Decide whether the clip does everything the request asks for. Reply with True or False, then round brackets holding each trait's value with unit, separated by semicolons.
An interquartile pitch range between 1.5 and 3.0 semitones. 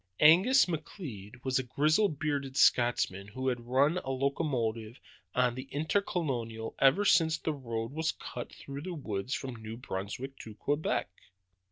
False (4.8 semitones)